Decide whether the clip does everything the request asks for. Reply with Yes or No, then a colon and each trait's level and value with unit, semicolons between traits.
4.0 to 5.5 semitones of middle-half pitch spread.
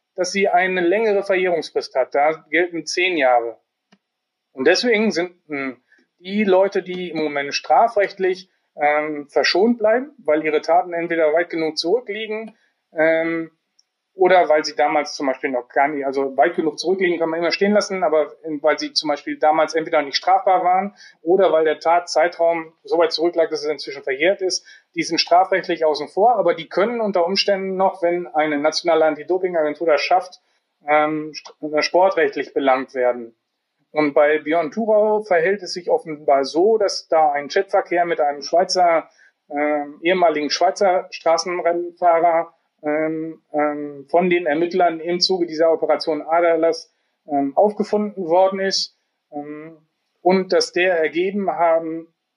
No: average, 3.4 semitones